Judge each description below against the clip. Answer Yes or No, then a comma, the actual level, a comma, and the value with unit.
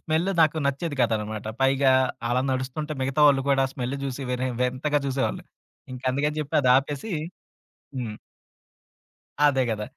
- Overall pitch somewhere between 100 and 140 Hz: Yes, low, 135 Hz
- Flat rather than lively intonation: Yes, narrow, 2.3 semitones